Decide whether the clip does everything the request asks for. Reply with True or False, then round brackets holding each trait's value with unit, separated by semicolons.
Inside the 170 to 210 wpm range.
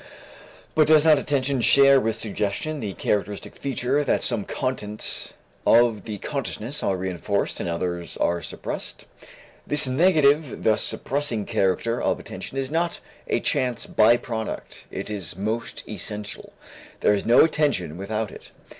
False (140 wpm)